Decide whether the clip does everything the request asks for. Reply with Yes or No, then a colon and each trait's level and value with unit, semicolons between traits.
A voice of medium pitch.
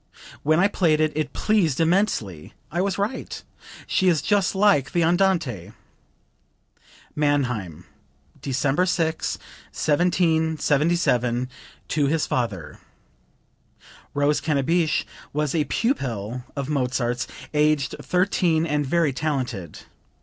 Yes: medium, 150 Hz